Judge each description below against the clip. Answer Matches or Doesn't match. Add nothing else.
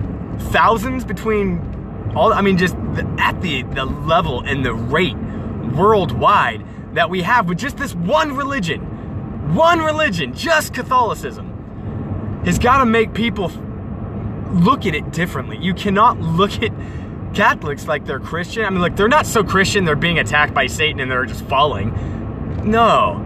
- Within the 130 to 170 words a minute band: Matches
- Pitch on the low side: Doesn't match